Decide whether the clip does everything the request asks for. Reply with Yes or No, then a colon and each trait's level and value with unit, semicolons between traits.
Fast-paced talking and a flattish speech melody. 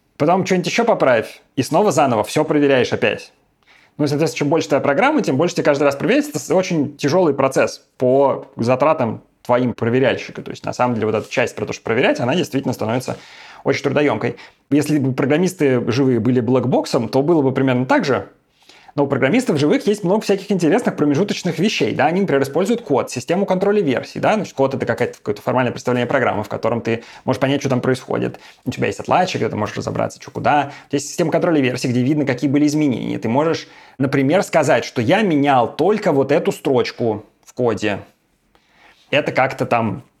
No: fast, 195 wpm; average, 4.5 semitones